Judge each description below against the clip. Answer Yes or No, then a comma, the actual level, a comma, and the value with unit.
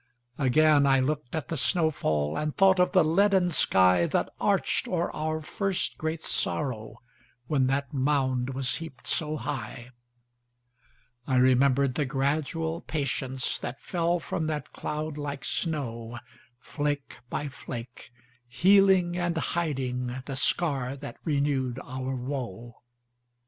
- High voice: No, medium, 140 Hz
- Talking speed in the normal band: No, slow, 110 wpm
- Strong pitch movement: No, average, 4.0 semitones